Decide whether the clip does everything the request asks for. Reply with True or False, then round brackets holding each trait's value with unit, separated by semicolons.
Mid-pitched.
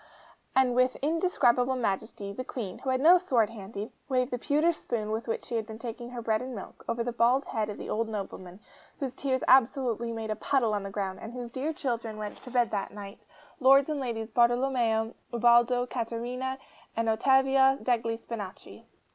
False (235 Hz)